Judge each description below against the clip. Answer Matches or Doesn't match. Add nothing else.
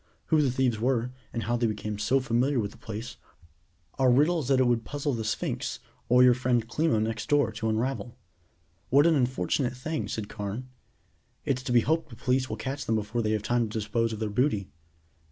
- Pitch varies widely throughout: Doesn't match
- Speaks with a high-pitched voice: Doesn't match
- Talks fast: Matches